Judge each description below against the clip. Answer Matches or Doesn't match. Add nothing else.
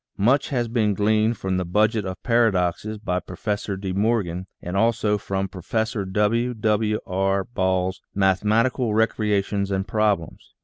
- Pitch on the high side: Doesn't match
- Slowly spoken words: Doesn't match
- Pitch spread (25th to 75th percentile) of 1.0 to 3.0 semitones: Matches